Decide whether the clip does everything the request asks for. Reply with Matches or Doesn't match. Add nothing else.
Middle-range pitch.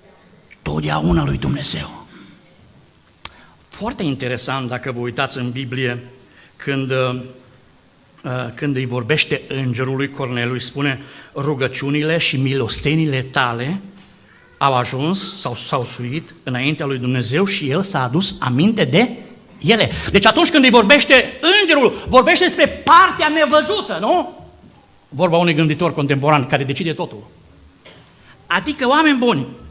Matches